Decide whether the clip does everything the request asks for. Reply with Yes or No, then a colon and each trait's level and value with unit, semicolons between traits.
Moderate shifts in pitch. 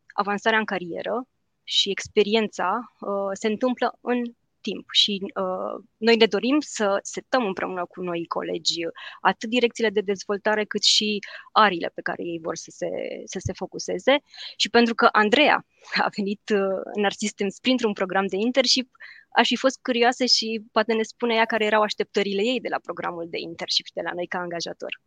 Yes: average, 3.2 semitones